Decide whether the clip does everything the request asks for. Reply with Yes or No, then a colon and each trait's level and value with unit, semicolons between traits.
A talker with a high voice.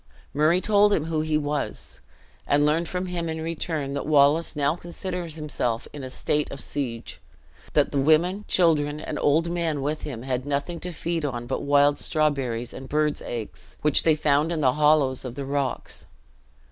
No: medium, 150 Hz